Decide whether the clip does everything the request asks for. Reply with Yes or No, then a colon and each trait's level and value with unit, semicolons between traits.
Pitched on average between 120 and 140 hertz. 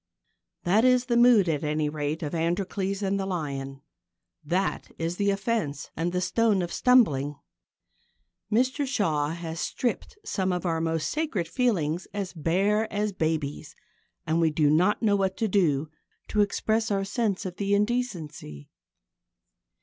No: medium, 185 Hz